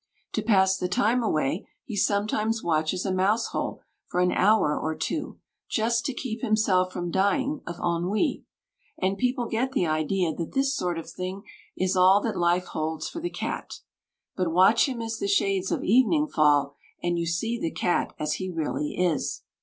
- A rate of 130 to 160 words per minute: No, average, 185 wpm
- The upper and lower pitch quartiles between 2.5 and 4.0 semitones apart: No, average, 4.6 semitones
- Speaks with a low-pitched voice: No, high, 190 Hz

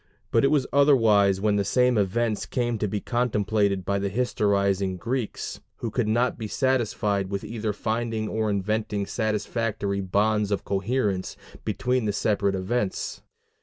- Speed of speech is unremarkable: Yes, average, 150 wpm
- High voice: No, low, 105 Hz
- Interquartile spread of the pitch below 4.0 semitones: Yes, average, 2.9 semitones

